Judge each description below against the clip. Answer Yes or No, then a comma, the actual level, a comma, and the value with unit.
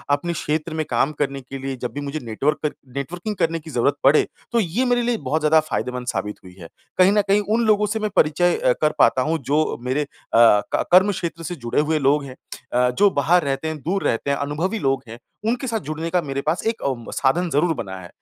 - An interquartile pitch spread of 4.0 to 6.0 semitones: Yes, average, 4.7 semitones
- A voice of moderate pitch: Yes, medium, 150 Hz